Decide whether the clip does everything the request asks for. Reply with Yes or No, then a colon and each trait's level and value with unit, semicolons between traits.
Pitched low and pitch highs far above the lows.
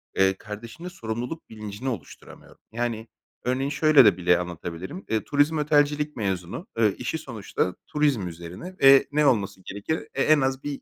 Yes: low, 120 Hz; wide, 6.7 semitones